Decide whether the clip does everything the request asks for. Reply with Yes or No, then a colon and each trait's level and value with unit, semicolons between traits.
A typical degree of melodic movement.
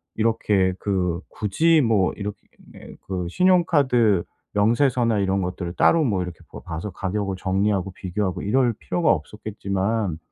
Yes: average, 3.5 semitones